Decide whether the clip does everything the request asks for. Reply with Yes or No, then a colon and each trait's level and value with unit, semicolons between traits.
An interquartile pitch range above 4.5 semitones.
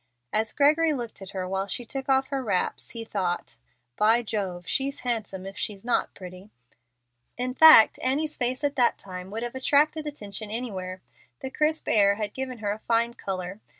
Yes: average, 5.2 semitones